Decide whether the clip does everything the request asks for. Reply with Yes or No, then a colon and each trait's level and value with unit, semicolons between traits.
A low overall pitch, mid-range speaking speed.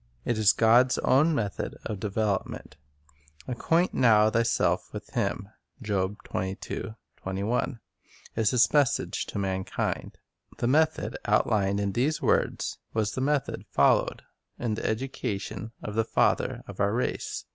No: low, 110 Hz; slow, 125 wpm